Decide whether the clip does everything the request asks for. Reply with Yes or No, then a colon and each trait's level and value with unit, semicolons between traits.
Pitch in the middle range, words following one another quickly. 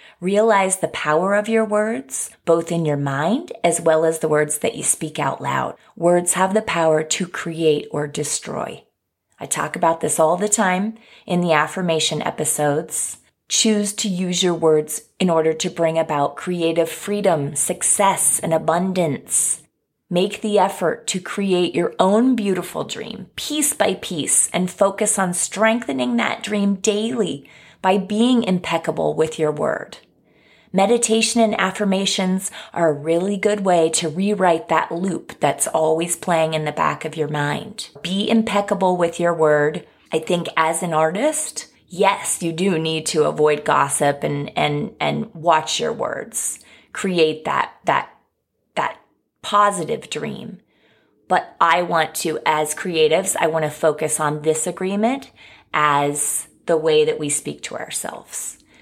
No: medium, 170 Hz; average, 155 wpm